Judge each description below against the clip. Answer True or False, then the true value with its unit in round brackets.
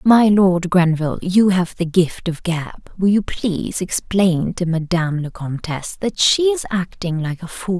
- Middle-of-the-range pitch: True (180 Hz)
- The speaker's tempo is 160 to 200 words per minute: True (185 wpm)